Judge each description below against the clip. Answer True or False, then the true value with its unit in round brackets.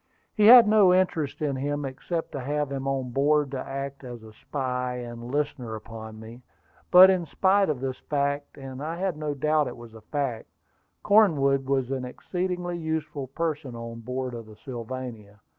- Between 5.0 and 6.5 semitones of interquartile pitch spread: False (3.7 semitones)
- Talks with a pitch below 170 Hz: True (135 Hz)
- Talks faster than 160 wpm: True (180 wpm)